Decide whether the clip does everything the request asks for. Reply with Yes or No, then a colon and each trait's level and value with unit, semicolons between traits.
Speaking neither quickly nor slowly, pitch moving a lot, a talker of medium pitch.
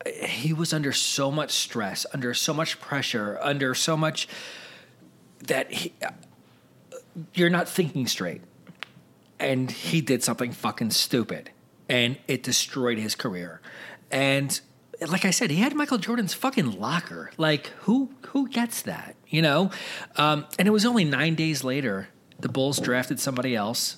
Yes: average, 155 wpm; wide, 6.5 semitones; medium, 150 Hz